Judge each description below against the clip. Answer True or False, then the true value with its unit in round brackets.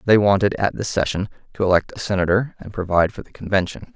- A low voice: True (95 Hz)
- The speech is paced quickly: True (215 wpm)